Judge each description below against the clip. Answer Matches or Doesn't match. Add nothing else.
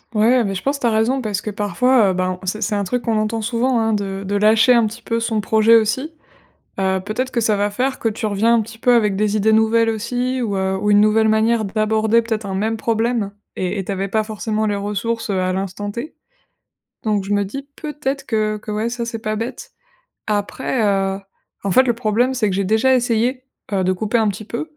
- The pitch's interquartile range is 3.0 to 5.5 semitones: Doesn't match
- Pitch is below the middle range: Doesn't match